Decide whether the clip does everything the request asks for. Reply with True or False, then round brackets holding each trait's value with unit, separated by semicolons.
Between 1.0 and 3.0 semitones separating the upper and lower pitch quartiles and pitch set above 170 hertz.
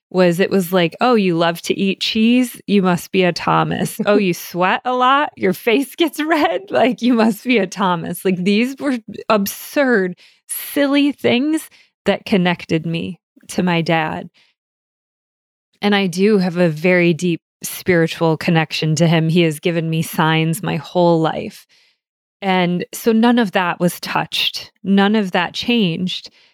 False (4.9 semitones; 190 Hz)